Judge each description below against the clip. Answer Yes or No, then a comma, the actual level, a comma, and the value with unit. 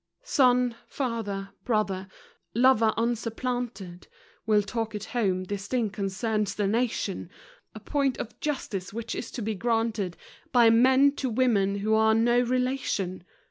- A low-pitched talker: No, high, 225 Hz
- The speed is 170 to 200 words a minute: No, average, 140 wpm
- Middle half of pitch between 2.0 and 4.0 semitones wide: Yes, average, 3.6 semitones